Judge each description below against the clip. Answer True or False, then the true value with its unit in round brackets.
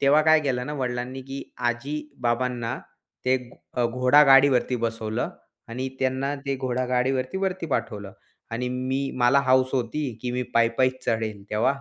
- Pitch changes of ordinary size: False (2.1 semitones)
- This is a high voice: False (130 Hz)